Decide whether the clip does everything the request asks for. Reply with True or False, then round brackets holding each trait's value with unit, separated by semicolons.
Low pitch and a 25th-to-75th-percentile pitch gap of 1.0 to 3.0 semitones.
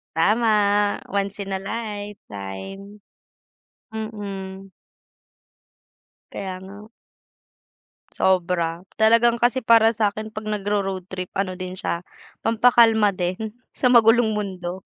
False (205 Hz; 2.6 semitones)